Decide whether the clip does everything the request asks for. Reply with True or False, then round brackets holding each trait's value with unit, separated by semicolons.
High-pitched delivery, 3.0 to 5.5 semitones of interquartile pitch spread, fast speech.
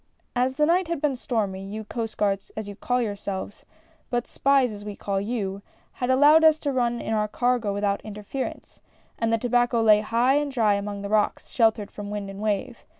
True (225 Hz; 3.5 semitones; 210 wpm)